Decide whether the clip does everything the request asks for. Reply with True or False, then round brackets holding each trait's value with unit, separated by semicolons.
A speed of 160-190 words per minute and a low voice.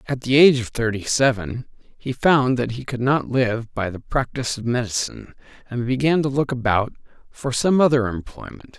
True (185 wpm; 125 Hz)